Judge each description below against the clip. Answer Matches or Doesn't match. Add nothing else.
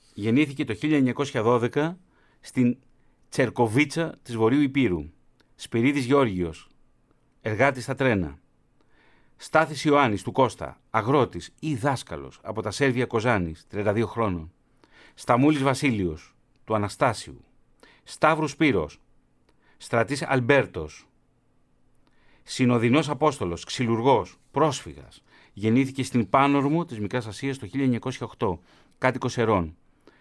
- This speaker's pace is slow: Matches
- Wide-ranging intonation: Doesn't match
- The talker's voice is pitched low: Matches